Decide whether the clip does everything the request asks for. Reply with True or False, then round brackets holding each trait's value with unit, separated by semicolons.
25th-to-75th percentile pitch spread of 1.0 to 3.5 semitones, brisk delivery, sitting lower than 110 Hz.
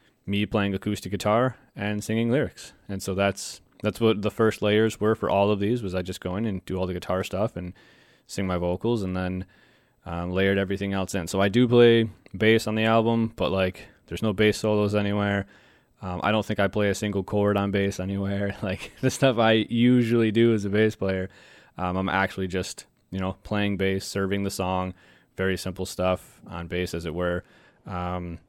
True (2.6 semitones; 210 wpm; 100 Hz)